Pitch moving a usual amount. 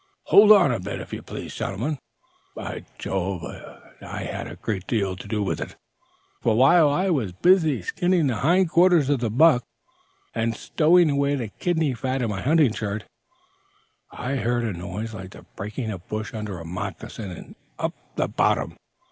No: wide, 6.9 semitones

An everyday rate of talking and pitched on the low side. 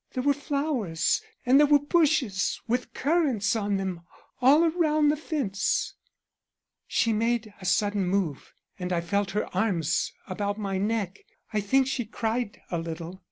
No: average, 155 wpm; high, 215 Hz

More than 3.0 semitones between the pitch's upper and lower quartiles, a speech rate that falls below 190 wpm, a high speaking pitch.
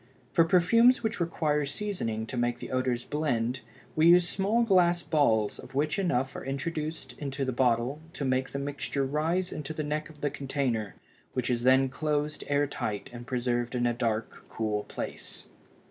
No: average, 4.3 semitones; average, 175 wpm; medium, 140 Hz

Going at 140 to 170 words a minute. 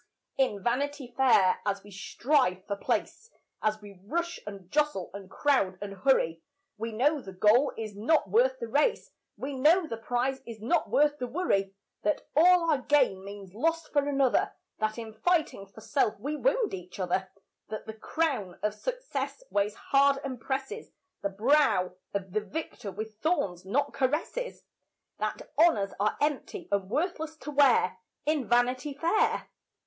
Yes: average, 165 wpm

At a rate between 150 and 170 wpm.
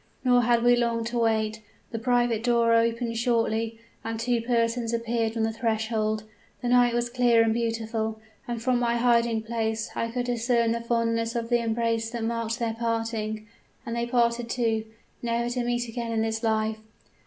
No: average, 180 wpm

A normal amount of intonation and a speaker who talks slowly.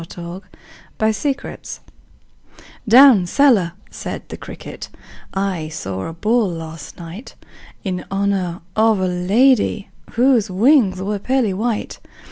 Yes: average, 4.6 semitones; slow, 115 wpm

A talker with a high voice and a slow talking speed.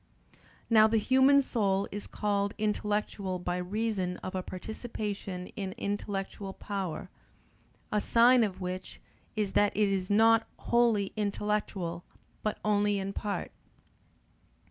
Yes: high, 205 Hz; slow, 120 wpm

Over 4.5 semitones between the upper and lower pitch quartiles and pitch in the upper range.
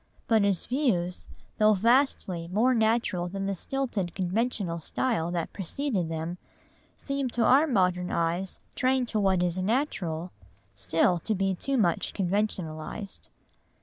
Yes: average, 5.1 semitones; high, 195 Hz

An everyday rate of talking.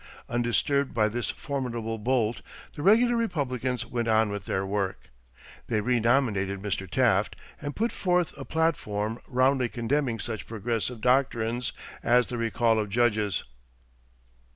No: slow, 130 wpm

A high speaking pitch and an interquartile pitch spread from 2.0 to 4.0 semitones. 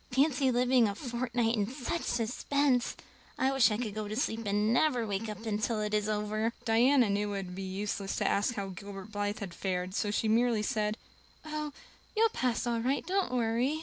Yes: high, 225 Hz; average, 3.3 semitones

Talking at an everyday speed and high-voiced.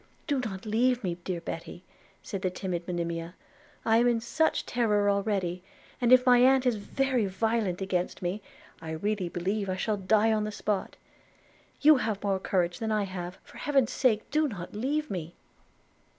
Yes: average, 180 wpm; high, 210 Hz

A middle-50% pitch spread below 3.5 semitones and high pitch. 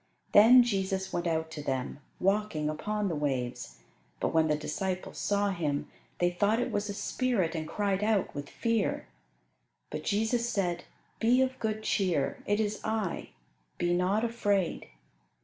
No: average, 4.6 semitones; high, 195 Hz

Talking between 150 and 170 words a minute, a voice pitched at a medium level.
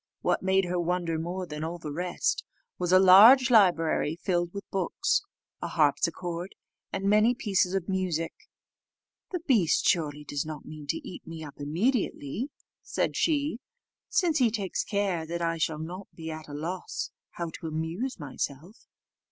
Yes: average, 160 wpm; medium, 175 Hz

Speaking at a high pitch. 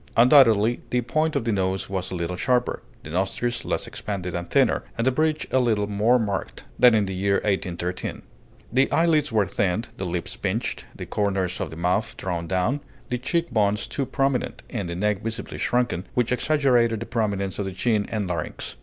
No: low, 105 Hz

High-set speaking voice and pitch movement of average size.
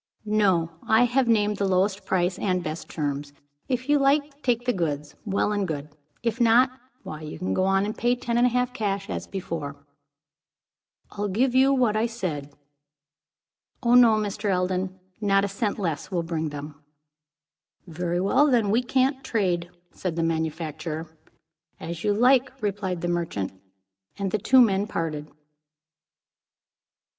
No: high, 195 Hz; wide, 5.8 semitones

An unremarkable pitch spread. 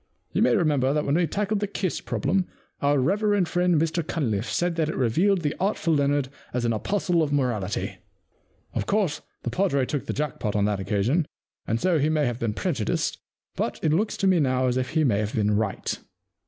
No: wide, 6.2 semitones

